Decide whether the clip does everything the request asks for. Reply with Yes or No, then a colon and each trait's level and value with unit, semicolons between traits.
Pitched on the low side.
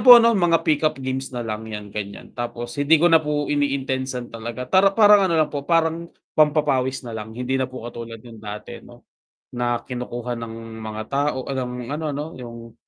Yes: low, 130 Hz